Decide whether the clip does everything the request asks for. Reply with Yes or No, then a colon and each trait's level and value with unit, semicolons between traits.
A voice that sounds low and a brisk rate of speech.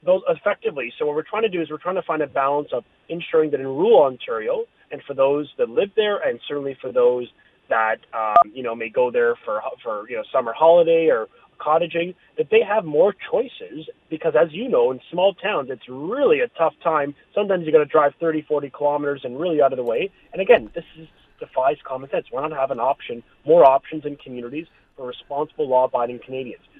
No: medium, 170 Hz; fast, 220 wpm